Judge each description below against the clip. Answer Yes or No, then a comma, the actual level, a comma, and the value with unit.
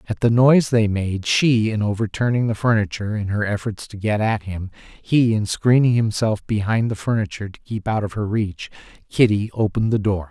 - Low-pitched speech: Yes, low, 105 Hz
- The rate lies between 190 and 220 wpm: Yes, average, 200 wpm